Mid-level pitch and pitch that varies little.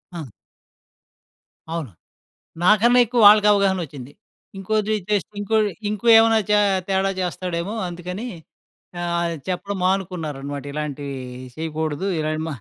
No: medium, 180 Hz; average, 4.8 semitones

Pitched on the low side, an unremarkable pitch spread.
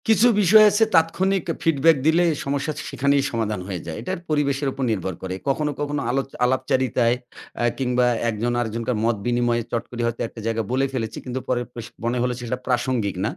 Yes: low, 125 Hz; average, 3.6 semitones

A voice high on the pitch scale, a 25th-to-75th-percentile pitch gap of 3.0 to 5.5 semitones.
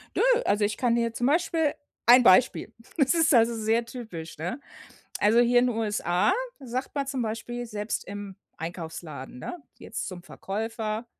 Yes: high, 225 Hz; average, 3.3 semitones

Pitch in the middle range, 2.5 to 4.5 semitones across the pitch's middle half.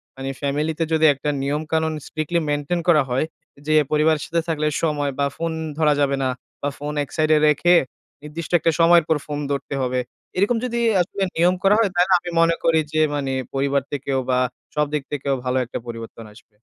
Yes: medium, 150 Hz; average, 3.0 semitones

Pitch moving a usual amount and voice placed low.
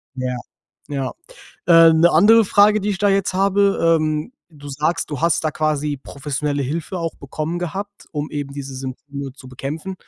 No: average, 4.7 semitones; medium, 155 Hz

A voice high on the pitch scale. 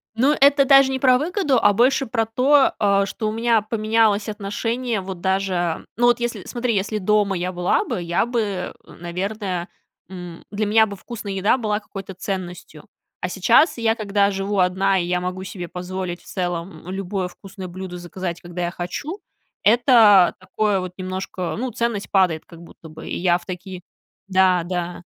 Yes: high, 195 Hz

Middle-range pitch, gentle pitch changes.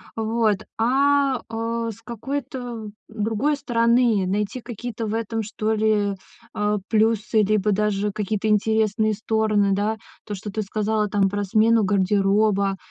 No: high, 215 Hz; narrow, 1.7 semitones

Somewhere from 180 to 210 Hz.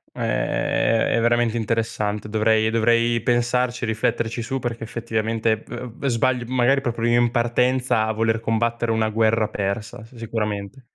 No: low, 115 Hz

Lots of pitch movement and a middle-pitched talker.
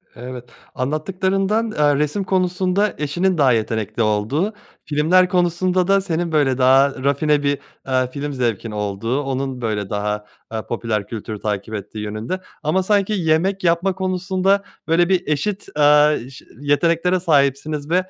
Yes: wide, 6.5 semitones; medium, 150 Hz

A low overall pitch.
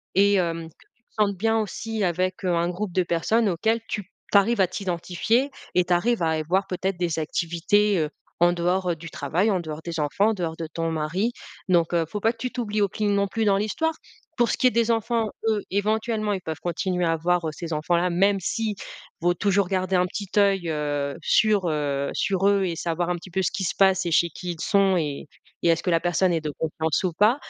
No: medium, 185 Hz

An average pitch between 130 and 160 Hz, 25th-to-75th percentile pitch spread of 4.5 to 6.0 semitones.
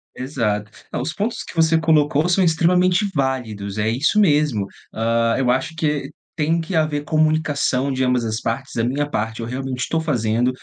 Yes: medium, 140 Hz; average, 5.3 semitones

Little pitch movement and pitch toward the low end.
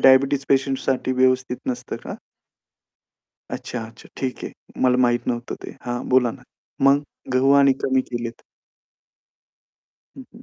Yes: narrow, 1.6 semitones; low, 130 Hz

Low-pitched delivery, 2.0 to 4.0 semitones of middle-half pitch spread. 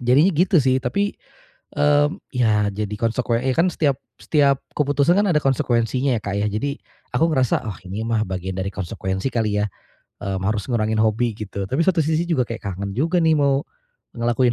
No: low, 125 Hz; wide, 5.4 semitones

